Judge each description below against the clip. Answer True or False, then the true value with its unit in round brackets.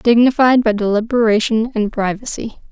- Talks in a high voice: True (225 Hz)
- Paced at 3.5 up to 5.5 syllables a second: True (5.2 syllables/s)